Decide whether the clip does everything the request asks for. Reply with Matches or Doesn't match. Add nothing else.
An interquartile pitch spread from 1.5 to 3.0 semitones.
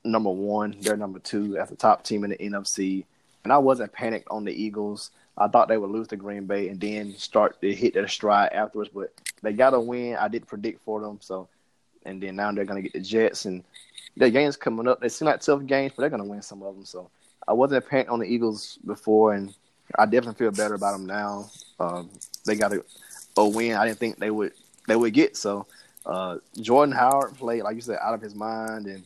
Matches